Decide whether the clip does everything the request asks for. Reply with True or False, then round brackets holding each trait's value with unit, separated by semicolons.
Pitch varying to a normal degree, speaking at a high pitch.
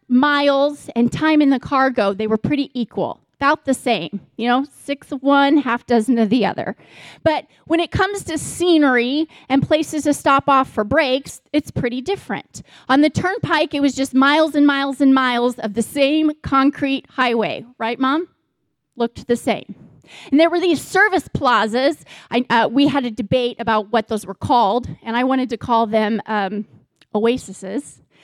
True (3.7 semitones; 265 Hz)